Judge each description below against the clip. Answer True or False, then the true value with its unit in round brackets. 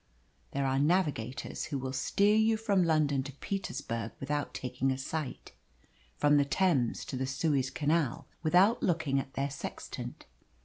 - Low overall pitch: False (145 Hz)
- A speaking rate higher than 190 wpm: False (150 wpm)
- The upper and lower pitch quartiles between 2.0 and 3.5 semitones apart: False (4.1 semitones)